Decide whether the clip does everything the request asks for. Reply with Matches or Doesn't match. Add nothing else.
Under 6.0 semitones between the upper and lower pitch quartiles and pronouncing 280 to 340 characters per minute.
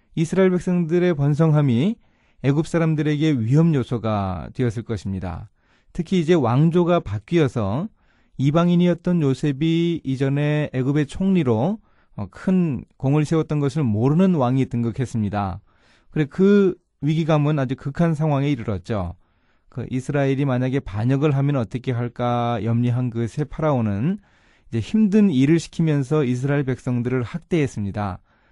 Matches